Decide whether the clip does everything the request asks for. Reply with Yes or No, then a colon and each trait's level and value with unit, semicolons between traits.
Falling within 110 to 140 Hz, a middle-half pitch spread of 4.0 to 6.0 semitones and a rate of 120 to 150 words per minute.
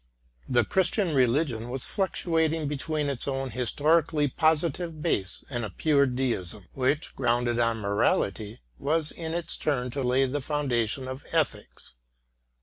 Yes: low, 135 Hz; average, 4.4 semitones; average, 145 wpm